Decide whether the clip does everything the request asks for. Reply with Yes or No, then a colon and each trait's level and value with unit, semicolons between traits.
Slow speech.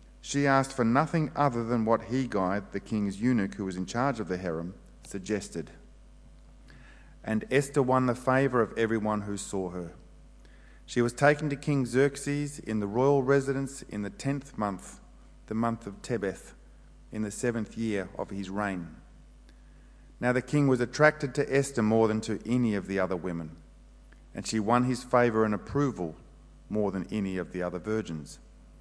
No: average, 175 wpm